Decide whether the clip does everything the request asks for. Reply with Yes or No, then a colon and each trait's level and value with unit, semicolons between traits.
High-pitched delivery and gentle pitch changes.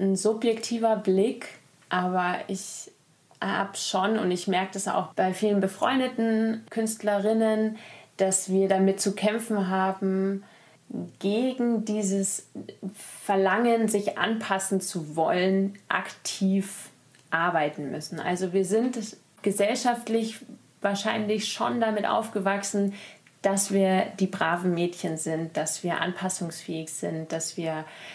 No: high, 195 Hz; average, 3.0 semitones